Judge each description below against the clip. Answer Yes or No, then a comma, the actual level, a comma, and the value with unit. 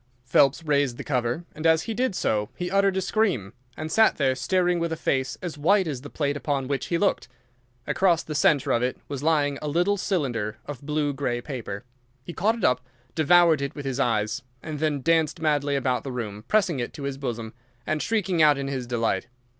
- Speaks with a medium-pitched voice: Yes, medium, 145 Hz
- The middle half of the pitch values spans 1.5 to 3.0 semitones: No, average, 4.7 semitones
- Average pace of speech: No, fast, 215 wpm